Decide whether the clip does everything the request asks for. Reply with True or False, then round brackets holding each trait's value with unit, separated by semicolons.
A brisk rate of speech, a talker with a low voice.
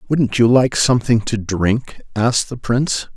False (170 wpm; 120 Hz)